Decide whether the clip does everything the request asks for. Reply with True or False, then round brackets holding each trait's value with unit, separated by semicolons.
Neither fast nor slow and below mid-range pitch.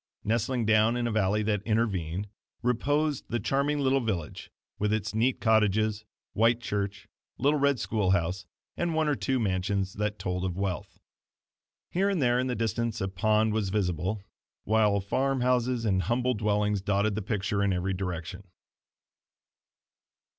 True (155 wpm; 110 Hz)